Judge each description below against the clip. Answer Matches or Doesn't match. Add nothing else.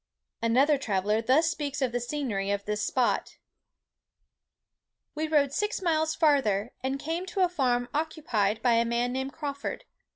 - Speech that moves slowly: Doesn't match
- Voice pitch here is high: Matches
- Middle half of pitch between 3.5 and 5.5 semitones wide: Matches